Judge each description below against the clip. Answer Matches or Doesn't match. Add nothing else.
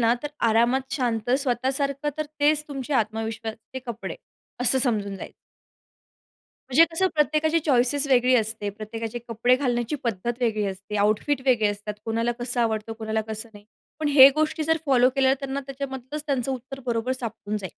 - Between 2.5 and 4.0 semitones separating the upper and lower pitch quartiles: Matches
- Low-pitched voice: Doesn't match